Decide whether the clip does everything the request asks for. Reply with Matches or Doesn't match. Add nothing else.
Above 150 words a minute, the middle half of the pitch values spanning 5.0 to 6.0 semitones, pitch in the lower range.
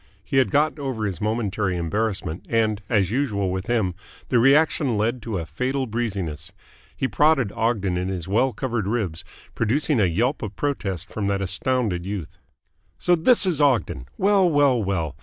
Matches